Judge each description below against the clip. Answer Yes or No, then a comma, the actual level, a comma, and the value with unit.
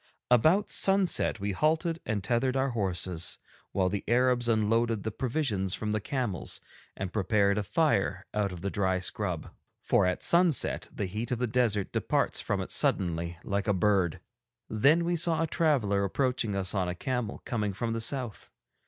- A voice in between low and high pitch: No, low, 110 Hz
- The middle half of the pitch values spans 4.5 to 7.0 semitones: Yes, average, 4.8 semitones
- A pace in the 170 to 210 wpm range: Yes, average, 175 wpm